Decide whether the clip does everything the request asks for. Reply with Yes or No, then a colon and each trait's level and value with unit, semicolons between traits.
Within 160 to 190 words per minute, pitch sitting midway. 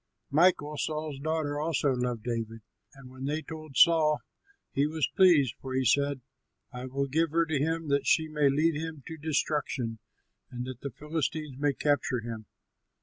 Yes: average, 170 wpm; medium, 145 Hz